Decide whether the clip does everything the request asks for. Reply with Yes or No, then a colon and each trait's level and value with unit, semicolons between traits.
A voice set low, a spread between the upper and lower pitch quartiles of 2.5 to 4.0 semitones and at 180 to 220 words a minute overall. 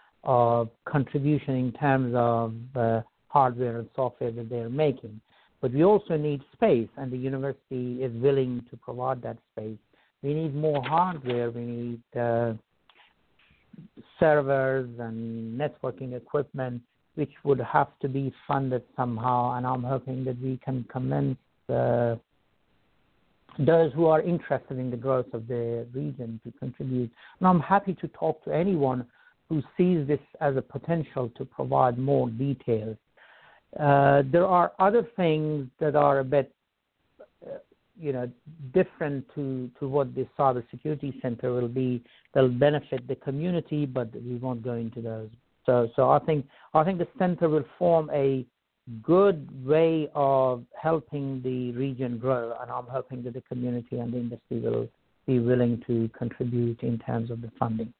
No: low, 130 Hz; average, 3.3 semitones; average, 155 wpm